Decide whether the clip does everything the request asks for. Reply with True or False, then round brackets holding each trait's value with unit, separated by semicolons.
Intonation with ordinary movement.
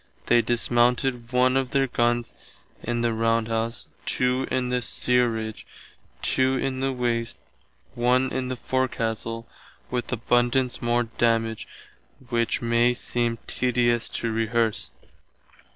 False (1.4 semitones)